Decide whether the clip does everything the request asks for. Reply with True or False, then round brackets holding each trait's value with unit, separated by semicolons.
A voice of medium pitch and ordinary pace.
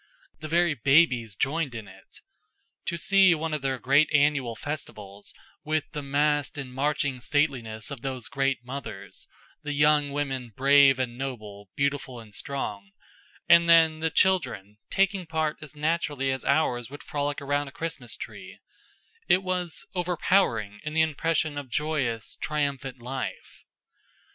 True (145 Hz; 145 wpm)